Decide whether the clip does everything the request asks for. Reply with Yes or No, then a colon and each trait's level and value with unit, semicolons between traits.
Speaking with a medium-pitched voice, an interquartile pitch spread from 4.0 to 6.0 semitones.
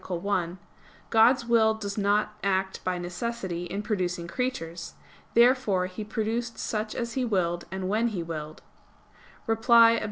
No: high, 205 Hz; average, 4.4 semitones